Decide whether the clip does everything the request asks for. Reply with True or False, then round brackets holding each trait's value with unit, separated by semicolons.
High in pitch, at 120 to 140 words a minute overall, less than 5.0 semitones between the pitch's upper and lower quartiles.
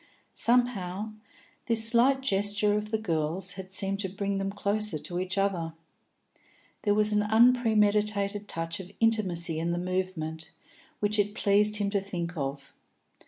False (200 Hz; 150 wpm; 2.8 semitones)